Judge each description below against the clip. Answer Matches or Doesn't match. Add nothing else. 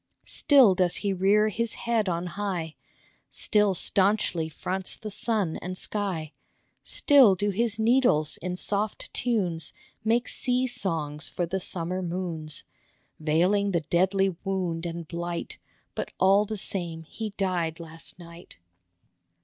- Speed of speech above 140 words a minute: Doesn't match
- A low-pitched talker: Doesn't match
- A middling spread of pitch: Matches